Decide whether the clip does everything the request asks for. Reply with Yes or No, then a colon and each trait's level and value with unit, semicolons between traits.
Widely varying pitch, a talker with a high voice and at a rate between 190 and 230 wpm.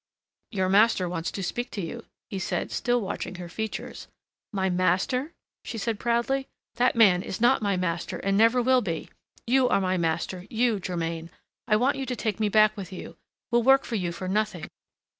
No: average, 4.6 semitones; high, 205 Hz; average, 195 wpm